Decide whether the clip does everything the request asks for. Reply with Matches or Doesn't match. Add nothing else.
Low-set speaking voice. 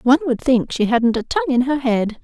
Doesn't match